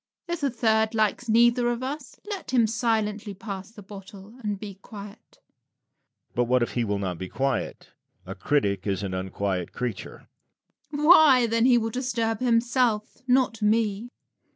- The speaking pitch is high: Yes, high, 220 Hz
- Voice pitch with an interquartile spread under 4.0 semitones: No, average, 4.3 semitones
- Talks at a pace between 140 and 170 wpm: Yes, average, 165 wpm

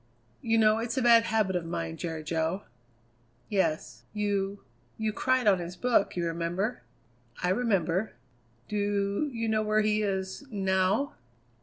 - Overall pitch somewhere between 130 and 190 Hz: No, high, 200 Hz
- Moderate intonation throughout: Yes, average, 3.5 semitones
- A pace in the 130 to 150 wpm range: Yes, average, 145 wpm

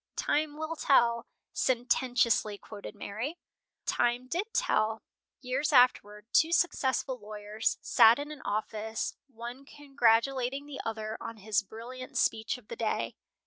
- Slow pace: Yes, slow, 130 wpm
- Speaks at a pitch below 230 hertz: No, high, 240 Hz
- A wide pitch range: No, average, 3.8 semitones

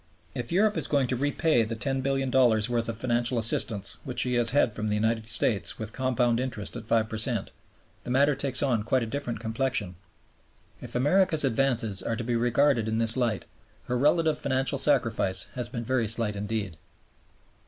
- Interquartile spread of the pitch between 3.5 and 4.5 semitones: No, average, 3.1 semitones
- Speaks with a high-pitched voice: No, low, 120 Hz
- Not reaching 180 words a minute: No, average, 185 wpm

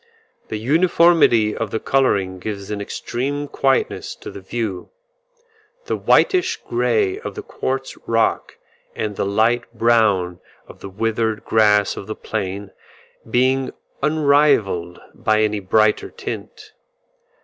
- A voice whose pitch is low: Yes, low, 110 Hz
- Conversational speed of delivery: No, slow, 125 wpm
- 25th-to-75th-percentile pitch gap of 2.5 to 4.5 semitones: No, average, 5.0 semitones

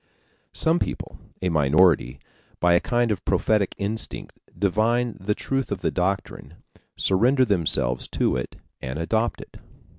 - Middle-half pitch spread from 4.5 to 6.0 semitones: Yes, average, 5.3 semitones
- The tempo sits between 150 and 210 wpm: No, average, 140 wpm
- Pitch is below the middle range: Yes, very low, 95 Hz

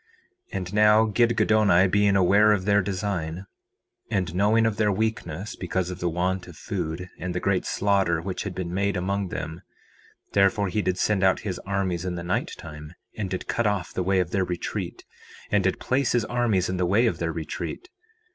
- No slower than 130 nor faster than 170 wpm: No, average, 200 wpm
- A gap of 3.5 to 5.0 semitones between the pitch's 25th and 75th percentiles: No, narrow, 2.5 semitones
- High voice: No, very low, 95 Hz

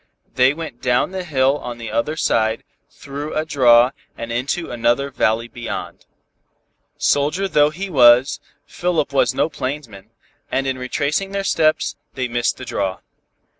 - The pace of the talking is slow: No, average, 150 wpm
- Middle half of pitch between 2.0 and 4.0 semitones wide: No, average, 4.4 semitones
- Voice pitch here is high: No, low, 135 Hz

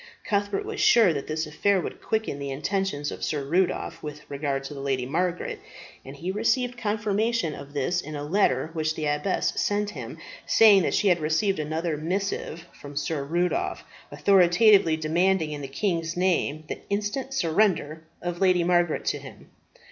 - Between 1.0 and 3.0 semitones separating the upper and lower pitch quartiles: No, average, 4.9 semitones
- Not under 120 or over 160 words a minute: No, average, 170 wpm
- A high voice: No, medium, 170 Hz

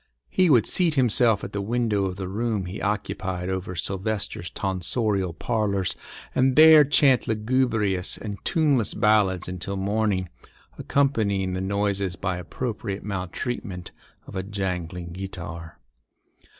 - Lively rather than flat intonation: No, average, 3.4 semitones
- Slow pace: Yes, slow, 125 wpm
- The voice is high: No, low, 100 Hz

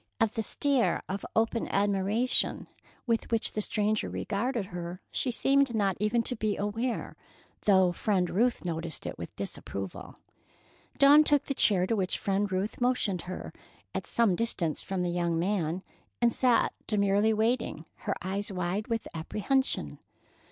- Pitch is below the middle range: No, high, 205 Hz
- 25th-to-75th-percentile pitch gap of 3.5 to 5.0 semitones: Yes, average, 3.9 semitones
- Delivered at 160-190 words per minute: No, average, 150 wpm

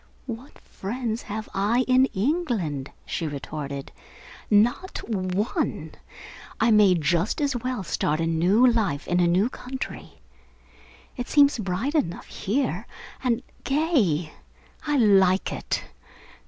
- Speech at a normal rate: No, slow, 120 wpm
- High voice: Yes, high, 215 Hz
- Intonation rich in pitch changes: Yes, wide, 6.2 semitones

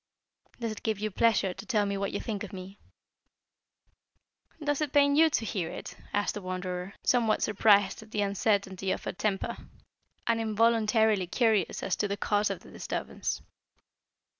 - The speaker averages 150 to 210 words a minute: Yes, average, 170 wpm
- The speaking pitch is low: No, high, 210 Hz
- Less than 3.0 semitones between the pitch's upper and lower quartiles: Yes, narrow, 2.5 semitones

